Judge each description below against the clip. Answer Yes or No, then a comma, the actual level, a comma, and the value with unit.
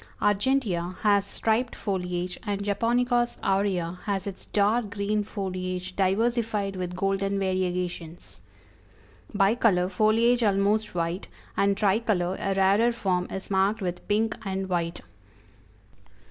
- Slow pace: Yes, slow, 115 wpm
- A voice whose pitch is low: No, high, 195 Hz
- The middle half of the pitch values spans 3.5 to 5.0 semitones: No, average, 2.7 semitones